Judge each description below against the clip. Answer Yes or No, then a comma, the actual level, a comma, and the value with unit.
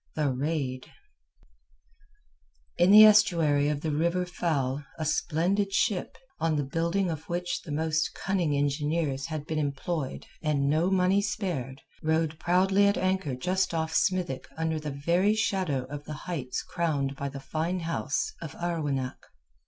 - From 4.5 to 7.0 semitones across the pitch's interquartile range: No, average, 3.8 semitones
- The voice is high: No, medium, 160 Hz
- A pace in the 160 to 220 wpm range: No, average, 150 wpm